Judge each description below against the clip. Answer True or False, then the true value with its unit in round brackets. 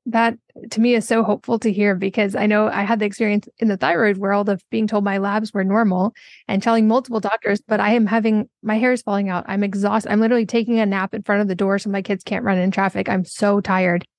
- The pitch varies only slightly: True (2.2 semitones)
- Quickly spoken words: True (260 wpm)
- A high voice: True (210 Hz)